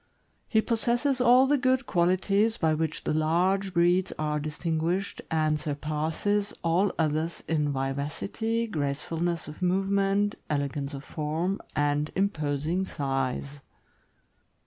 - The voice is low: No, medium, 165 Hz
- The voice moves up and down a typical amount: Yes, average, 4.8 semitones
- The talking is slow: Yes, slow, 115 wpm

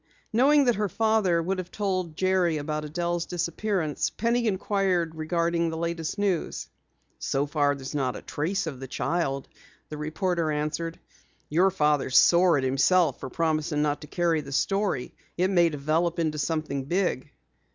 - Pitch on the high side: No, medium, 170 Hz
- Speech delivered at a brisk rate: No, average, 160 wpm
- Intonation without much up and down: No, average, 3.6 semitones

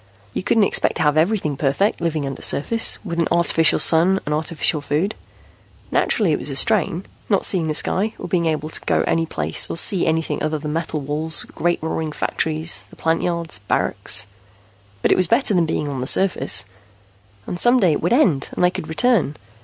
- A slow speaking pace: No, average, 195 wpm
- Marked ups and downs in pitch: No, average, 3.3 semitones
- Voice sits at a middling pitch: Yes, medium, 160 Hz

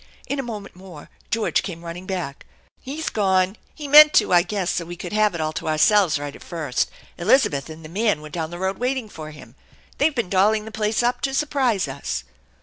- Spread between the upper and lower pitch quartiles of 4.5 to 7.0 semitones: Yes, wide, 5.6 semitones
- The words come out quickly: Yes, fast, 225 wpm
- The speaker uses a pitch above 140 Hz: Yes, high, 190 Hz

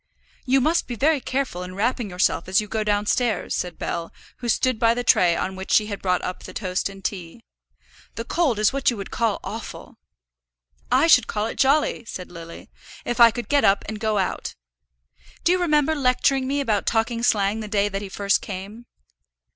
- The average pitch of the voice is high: Yes, high, 220 Hz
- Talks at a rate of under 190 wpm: No, average, 200 wpm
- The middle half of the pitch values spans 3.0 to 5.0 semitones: Yes, average, 4.4 semitones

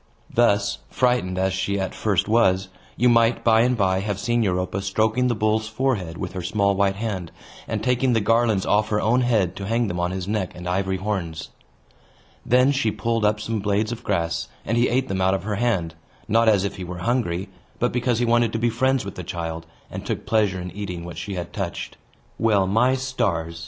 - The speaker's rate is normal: No, fast, 215 wpm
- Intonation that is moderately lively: Yes, average, 3.8 semitones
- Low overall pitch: Yes, low, 105 Hz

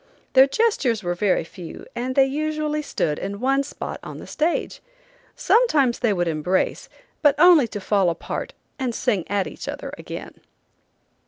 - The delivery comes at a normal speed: Yes, average, 160 wpm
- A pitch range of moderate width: No, wide, 7.2 semitones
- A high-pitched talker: Yes, very high, 250 Hz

